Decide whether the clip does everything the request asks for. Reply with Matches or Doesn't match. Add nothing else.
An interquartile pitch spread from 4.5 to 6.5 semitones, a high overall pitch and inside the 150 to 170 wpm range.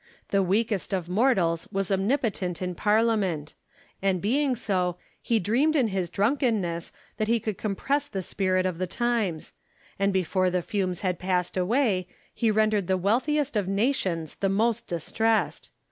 Doesn't match